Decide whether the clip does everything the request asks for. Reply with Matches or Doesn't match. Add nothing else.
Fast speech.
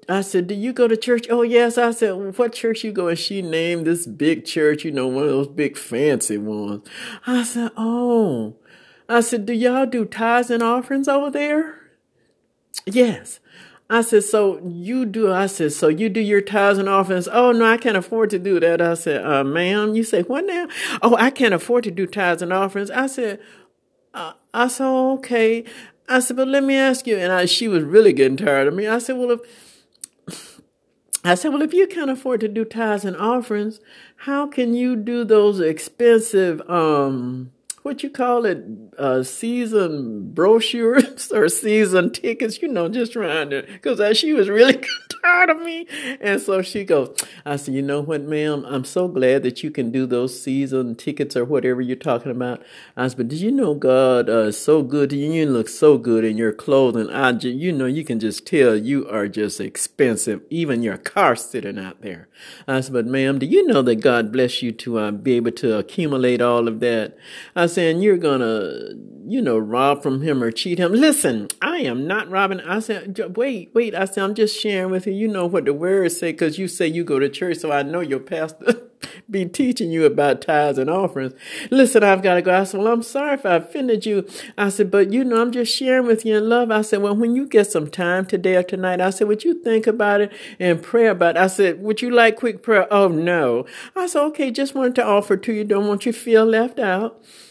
Matches